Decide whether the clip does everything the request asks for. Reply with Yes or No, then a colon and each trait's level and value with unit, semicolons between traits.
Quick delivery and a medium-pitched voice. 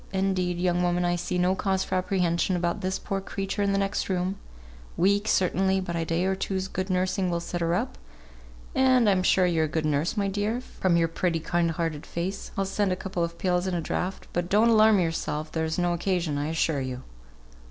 Yes: fast, 215 wpm; medium, 180 Hz